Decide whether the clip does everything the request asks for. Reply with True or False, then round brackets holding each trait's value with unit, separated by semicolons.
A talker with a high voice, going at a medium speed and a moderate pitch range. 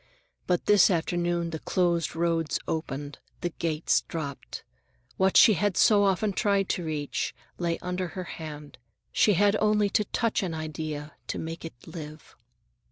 False (170 Hz; 155 wpm; 3.5 semitones)